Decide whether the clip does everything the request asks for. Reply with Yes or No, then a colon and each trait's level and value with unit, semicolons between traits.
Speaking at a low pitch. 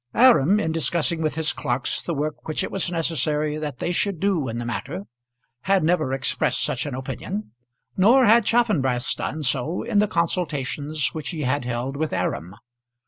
No: medium, 155 Hz